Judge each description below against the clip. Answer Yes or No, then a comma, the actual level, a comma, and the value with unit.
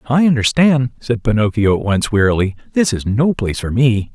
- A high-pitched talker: No, low, 120 Hz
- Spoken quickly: No, average, 190 wpm